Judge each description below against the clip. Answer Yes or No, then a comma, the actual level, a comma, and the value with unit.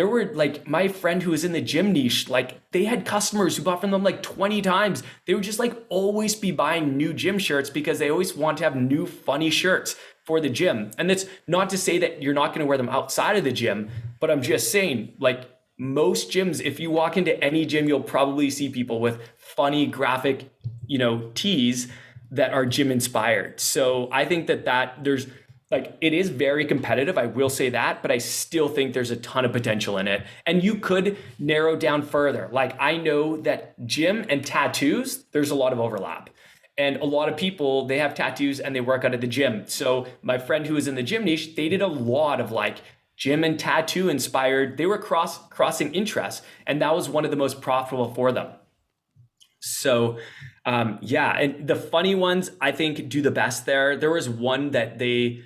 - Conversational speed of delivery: No, fast, 215 wpm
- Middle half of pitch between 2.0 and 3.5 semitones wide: No, average, 4.4 semitones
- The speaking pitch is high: No, medium, 145 Hz